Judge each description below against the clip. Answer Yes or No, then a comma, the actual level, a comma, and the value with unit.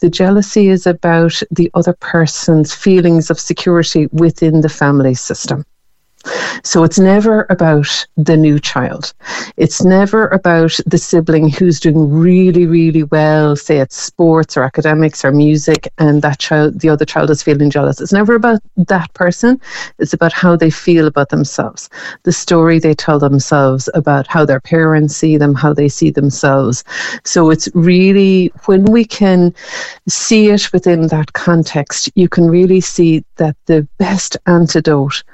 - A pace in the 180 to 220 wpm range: No, average, 155 wpm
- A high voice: No, medium, 165 Hz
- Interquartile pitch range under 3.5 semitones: Yes, average, 2.9 semitones